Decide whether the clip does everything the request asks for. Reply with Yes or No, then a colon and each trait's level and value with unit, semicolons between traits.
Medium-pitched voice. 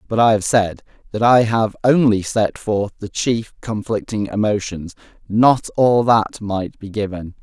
No: low, 105 Hz